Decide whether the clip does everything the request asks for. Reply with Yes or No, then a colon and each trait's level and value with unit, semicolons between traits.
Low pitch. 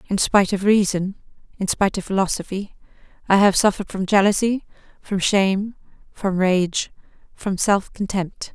No: high, 195 Hz